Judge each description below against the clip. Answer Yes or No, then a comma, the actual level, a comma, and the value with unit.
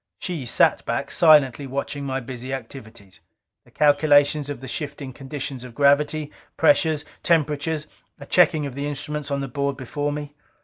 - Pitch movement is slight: Yes, narrow, 2.0 semitones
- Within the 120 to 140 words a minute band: No, average, 160 wpm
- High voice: No, medium, 145 Hz